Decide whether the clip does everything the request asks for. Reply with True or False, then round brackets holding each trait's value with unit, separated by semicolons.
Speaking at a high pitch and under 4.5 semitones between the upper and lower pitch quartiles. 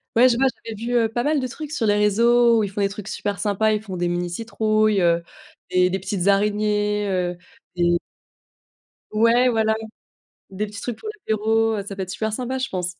True (210 Hz; 2.9 semitones)